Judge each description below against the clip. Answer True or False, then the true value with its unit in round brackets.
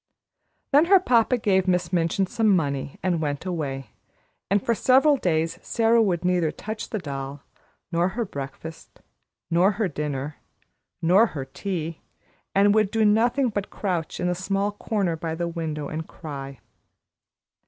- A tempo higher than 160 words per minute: False (155 wpm)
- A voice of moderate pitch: True (180 Hz)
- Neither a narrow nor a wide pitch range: True (4.9 semitones)